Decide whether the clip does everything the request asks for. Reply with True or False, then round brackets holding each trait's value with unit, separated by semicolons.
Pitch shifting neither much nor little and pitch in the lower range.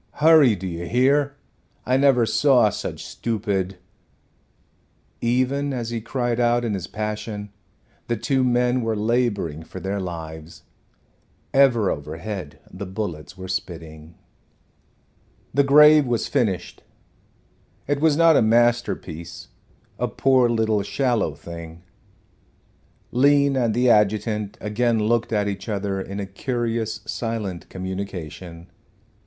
True (4.6 semitones; 110 Hz)